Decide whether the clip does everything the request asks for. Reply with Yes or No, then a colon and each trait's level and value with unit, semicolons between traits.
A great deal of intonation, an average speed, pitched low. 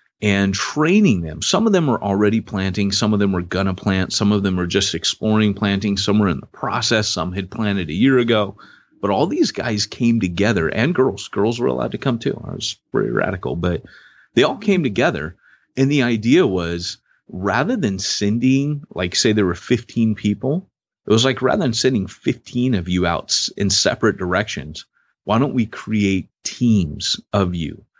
No: average, 3.7 semitones; average, 190 wpm; low, 105 Hz